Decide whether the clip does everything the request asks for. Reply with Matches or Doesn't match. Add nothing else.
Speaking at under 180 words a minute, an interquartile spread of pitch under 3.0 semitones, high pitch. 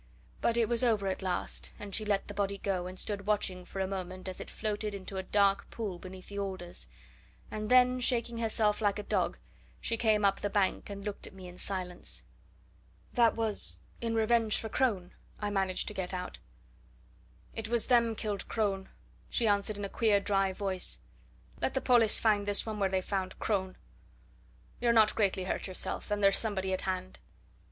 Doesn't match